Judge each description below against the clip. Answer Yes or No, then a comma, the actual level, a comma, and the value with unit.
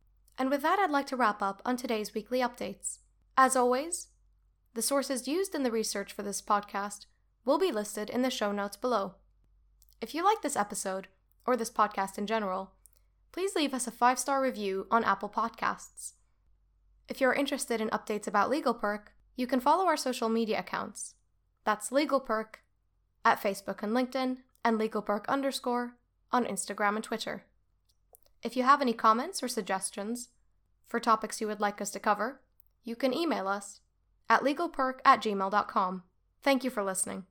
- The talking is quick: No, average, 165 wpm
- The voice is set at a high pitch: Yes, high, 230 Hz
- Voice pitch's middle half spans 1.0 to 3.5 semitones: No, average, 4.2 semitones